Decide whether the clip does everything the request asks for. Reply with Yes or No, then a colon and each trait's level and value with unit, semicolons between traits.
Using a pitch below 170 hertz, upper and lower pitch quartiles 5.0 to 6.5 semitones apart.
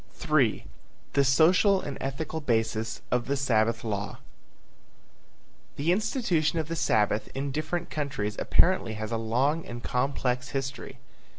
Yes: low, 135 Hz; wide, 5.4 semitones